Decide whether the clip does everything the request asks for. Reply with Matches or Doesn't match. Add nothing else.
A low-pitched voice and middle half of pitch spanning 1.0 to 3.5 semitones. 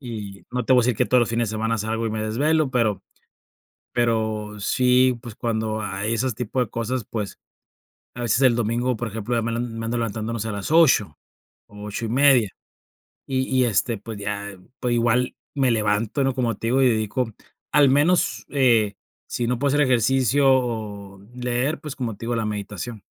Matches